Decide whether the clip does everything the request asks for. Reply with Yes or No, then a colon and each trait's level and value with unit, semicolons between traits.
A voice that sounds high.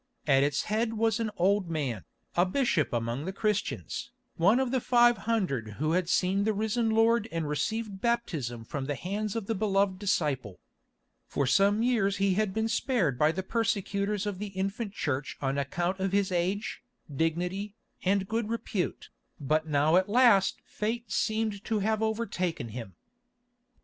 Yes: high, 195 Hz